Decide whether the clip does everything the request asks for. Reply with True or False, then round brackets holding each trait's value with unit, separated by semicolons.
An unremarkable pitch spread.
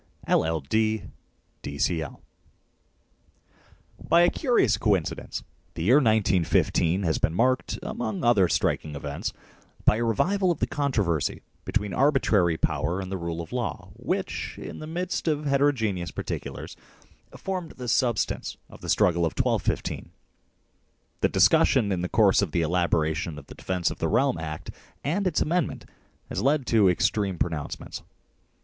False (8.2 semitones)